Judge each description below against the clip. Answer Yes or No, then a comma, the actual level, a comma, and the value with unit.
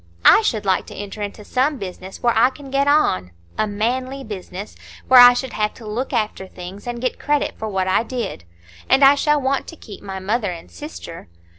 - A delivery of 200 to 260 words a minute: Yes, fast, 205 wpm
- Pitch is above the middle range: Yes, high, 220 Hz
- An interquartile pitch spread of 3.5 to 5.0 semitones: No, wide, 5.4 semitones